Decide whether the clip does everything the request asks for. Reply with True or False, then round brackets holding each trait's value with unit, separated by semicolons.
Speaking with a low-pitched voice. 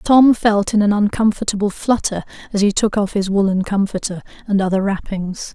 False (205 Hz)